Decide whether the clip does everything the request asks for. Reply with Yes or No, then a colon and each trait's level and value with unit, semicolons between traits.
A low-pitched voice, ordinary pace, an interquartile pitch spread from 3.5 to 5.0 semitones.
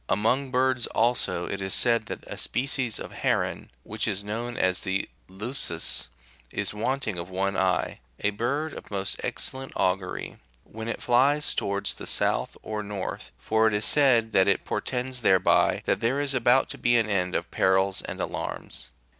Yes: low, 110 Hz; average, 175 wpm; average, 4.3 semitones